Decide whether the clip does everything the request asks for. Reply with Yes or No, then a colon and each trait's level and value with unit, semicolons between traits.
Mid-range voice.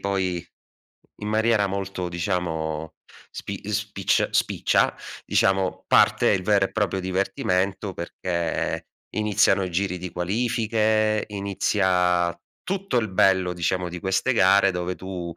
No: very low, 95 Hz